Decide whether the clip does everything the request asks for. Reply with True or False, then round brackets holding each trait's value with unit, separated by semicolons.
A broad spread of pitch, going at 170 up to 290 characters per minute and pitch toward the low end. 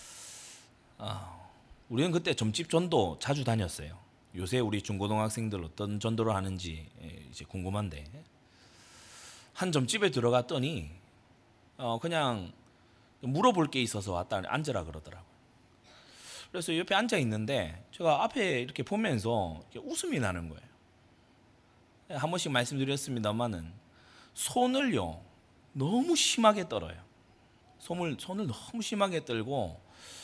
True (7.0 semitones; 270 characters per minute; 120 Hz)